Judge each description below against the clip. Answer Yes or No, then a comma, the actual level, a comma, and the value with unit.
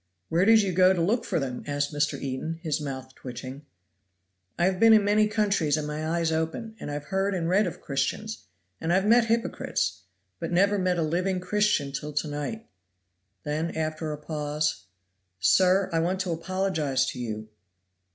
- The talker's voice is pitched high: No, medium, 165 Hz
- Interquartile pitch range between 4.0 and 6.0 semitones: Yes, average, 4.6 semitones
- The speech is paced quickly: No, average, 180 wpm